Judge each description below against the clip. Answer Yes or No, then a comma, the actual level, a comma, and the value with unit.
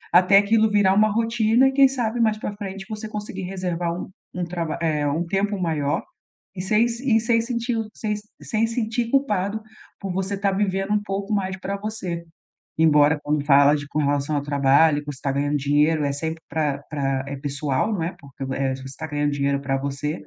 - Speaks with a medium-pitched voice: Yes, medium, 180 Hz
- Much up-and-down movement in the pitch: Yes, wide, 6.4 semitones